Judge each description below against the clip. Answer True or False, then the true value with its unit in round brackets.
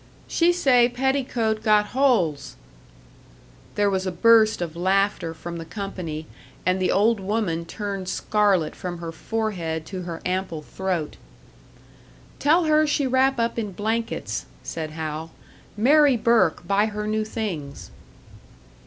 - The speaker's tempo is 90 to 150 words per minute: True (135 wpm)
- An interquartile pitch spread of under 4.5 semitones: False (5.0 semitones)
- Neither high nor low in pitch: False (205 Hz)